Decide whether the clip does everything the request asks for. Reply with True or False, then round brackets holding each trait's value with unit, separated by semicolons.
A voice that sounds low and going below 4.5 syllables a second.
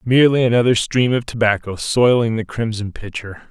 False (115 Hz; 5.4 syllables/s)